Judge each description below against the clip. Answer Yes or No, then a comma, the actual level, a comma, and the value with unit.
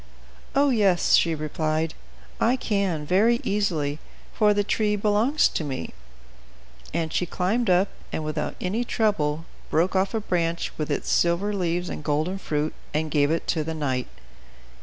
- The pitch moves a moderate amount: Yes, average, 5.0 semitones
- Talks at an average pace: Yes, average, 160 wpm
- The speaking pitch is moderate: Yes, medium, 175 Hz